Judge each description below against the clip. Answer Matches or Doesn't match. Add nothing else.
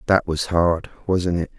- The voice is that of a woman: Doesn't match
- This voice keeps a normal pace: Matches